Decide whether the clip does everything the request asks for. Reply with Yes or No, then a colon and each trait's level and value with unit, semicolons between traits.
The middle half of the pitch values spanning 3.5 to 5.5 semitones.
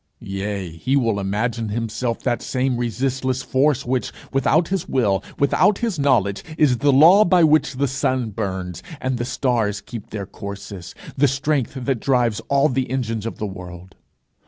Yes: average, 4.6 semitones